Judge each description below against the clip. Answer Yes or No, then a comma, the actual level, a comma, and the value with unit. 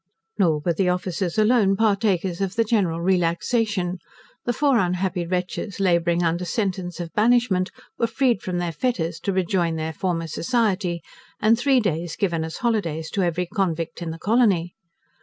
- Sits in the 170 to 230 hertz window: Yes, medium, 185 Hz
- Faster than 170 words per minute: No, average, 160 wpm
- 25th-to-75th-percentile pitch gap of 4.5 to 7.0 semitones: No, average, 3.7 semitones